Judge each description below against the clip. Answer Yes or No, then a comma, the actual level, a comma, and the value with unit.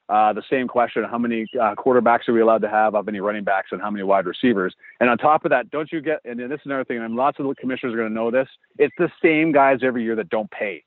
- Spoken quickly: Yes, fast, 300 wpm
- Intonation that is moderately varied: Yes, average, 3.6 semitones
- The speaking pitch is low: Yes, low, 120 Hz